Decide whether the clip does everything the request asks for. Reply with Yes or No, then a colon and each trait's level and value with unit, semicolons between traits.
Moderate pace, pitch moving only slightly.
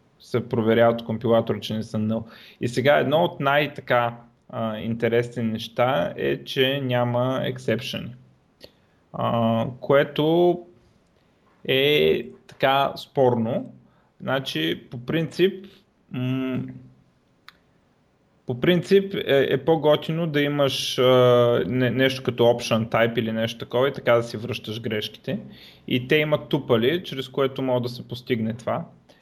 No: average, 125 wpm; average, 3.5 semitones